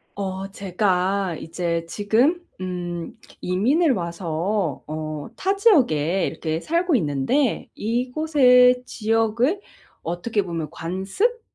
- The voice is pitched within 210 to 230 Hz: No, high, 200 Hz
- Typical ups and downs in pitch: No, wide, 6.6 semitones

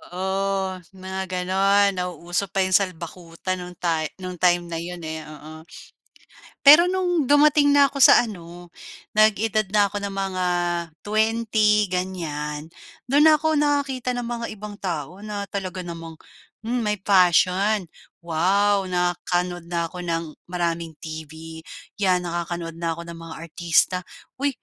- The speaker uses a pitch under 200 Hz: Yes, medium, 185 Hz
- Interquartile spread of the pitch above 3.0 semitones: Yes, average, 3.7 semitones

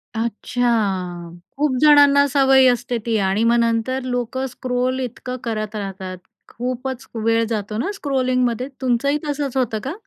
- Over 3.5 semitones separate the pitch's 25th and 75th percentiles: No, average, 3.0 semitones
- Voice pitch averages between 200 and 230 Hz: No, high, 245 Hz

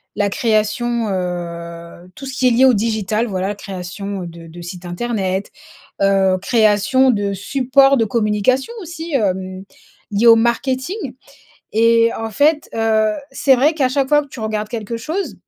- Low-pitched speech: No, high, 220 Hz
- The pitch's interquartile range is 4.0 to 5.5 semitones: Yes, average, 4.8 semitones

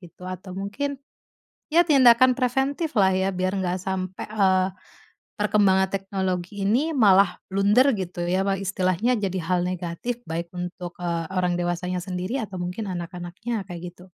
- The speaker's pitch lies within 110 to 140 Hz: No, high, 190 Hz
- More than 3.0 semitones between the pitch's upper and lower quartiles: No, average, 2.7 semitones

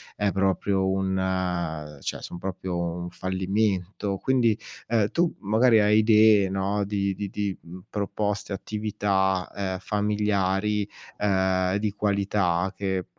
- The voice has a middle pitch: No, low, 100 Hz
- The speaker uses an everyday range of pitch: No, narrow, 1.9 semitones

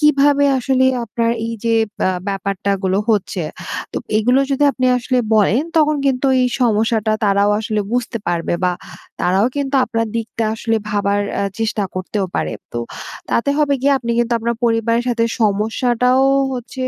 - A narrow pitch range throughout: No, average, 3.6 semitones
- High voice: Yes, high, 230 Hz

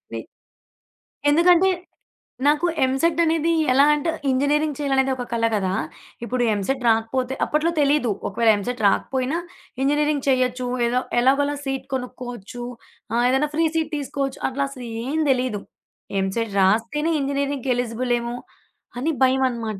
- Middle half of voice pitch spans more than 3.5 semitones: No, average, 3.2 semitones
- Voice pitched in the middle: No, very high, 265 Hz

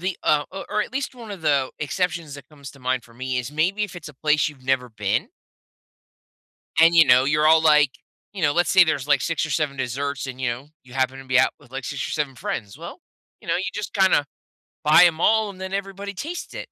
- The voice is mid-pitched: Yes, medium, 150 Hz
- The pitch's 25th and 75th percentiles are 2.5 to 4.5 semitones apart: No, average, 5.3 semitones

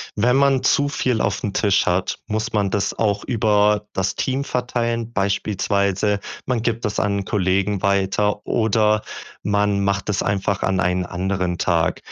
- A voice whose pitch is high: No, low, 105 Hz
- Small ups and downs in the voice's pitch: Yes, narrow, 2.2 semitones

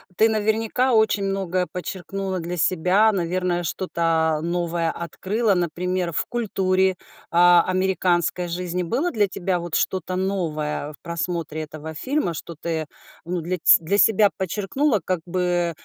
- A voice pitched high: No, medium, 180 Hz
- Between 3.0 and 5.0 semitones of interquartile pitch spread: No, narrow, 2.4 semitones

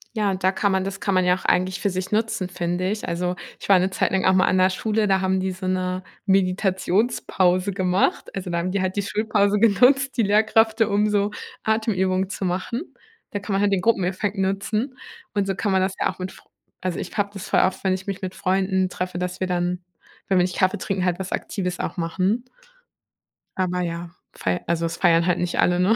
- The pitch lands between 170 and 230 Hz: Yes, high, 190 Hz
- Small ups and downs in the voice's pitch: Yes, narrow, 1.8 semitones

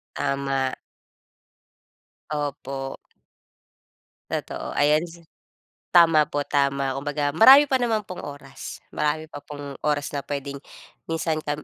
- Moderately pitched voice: Yes, medium, 145 Hz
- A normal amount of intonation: No, narrow, 2.3 semitones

